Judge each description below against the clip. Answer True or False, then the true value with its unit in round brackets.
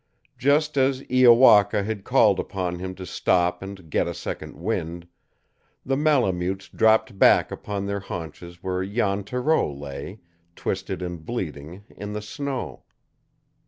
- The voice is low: True (100 Hz)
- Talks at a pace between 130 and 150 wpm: True (135 wpm)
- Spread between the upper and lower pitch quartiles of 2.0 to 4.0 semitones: False (4.8 semitones)